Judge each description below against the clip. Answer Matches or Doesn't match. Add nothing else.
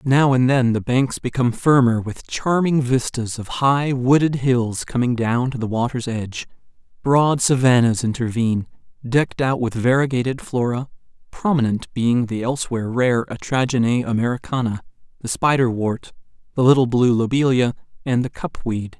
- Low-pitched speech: Matches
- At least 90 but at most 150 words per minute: Matches